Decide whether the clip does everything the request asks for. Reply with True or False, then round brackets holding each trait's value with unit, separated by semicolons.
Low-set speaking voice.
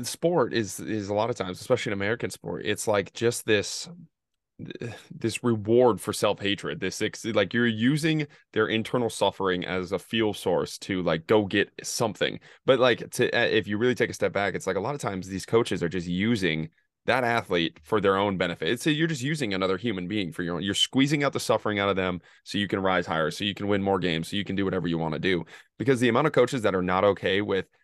True (105 Hz)